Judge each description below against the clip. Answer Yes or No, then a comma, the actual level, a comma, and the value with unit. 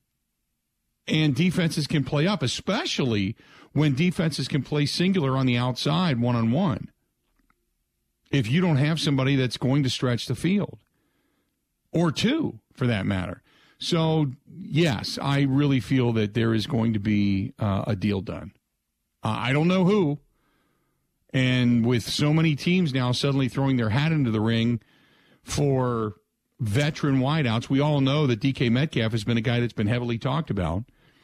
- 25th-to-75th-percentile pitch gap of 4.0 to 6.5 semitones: Yes, average, 4.3 semitones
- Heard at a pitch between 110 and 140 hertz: Yes, low, 135 Hz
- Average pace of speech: Yes, average, 160 wpm